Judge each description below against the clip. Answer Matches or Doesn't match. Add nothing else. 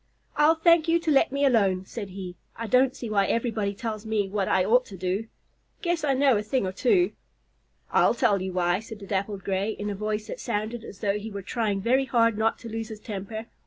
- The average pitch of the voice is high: Matches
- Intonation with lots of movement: Doesn't match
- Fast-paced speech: Matches